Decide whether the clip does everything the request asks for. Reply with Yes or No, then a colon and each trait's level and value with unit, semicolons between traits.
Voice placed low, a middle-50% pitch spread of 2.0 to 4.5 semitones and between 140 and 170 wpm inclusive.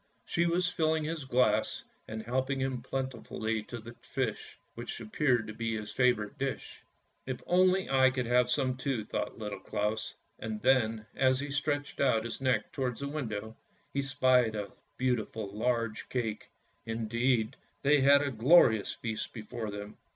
Yes: low, 125 Hz; average, 3.4 semitones; average, 165 wpm